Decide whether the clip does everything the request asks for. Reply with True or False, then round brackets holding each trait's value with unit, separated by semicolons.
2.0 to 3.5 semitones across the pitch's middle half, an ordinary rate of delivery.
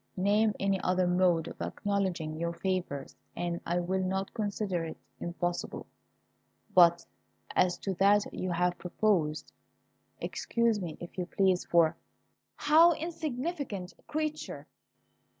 False (3.0 semitones; 125 wpm)